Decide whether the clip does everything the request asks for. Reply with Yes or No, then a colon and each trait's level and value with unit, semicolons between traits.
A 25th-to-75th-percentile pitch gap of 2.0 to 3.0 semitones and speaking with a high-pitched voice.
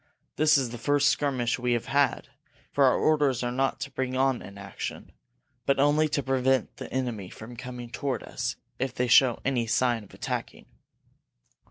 No: narrow, 2.4 semitones; low, 130 Hz